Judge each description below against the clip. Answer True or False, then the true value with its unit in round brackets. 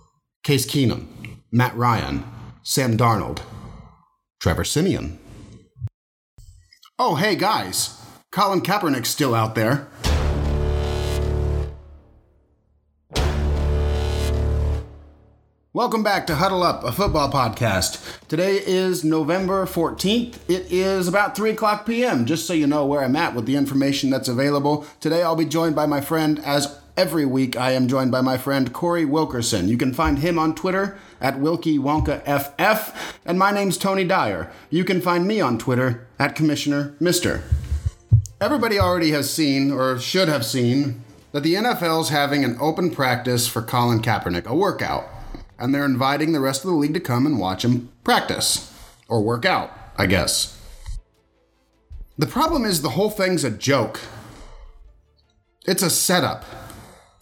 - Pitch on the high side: False (140 Hz)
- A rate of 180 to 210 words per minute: False (145 wpm)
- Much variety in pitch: True (7.0 semitones)